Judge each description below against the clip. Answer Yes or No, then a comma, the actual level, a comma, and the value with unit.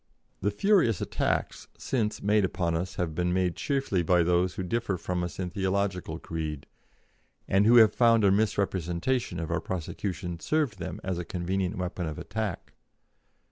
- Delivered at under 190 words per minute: Yes, average, 165 wpm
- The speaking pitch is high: No, very low, 95 Hz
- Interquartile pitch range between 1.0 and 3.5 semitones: Yes, average, 3.2 semitones